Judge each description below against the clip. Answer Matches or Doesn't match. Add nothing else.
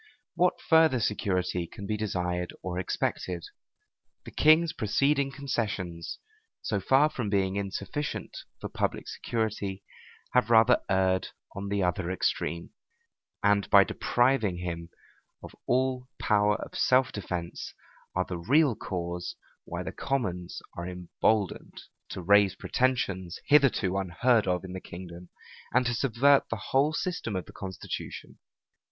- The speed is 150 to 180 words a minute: Doesn't match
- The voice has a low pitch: Matches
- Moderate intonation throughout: Doesn't match